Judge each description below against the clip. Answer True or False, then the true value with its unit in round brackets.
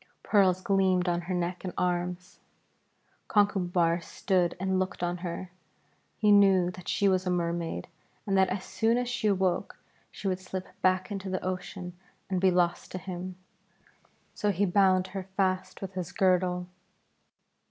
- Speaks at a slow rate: False (160 wpm)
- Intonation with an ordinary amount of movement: False (1.3 semitones)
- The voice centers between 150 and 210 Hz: True (185 Hz)